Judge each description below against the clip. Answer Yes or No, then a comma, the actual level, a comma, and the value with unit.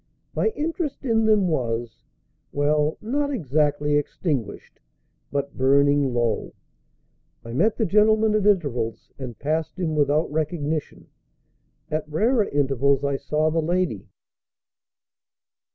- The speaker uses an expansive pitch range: Yes, wide, 5.8 semitones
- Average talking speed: No, slow, 115 wpm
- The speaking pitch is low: No, medium, 150 Hz